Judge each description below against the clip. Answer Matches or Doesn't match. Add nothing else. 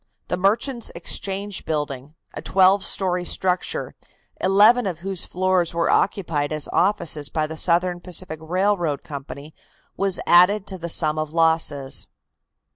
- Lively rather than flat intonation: Doesn't match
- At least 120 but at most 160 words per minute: Matches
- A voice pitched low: Doesn't match